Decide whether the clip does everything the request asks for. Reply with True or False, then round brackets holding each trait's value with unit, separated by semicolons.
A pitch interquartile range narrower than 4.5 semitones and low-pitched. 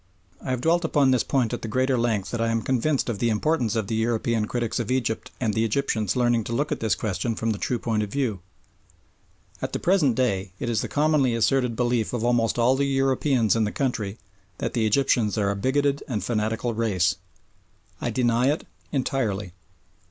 True (3.1 semitones; 120 Hz)